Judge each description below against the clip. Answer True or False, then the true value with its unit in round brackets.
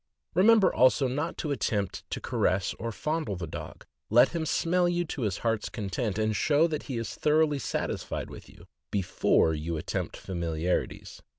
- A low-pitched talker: True (120 Hz)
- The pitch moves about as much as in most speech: False (8.3 semitones)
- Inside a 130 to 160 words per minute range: False (170 wpm)